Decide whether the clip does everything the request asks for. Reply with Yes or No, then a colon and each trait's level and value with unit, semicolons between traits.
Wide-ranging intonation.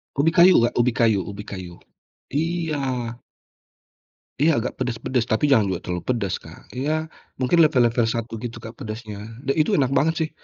Yes: wide, 5.7 semitones